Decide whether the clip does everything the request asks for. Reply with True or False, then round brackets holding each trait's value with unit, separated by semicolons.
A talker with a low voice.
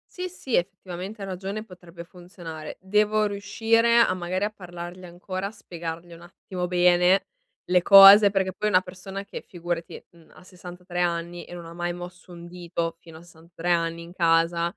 False (180 Hz)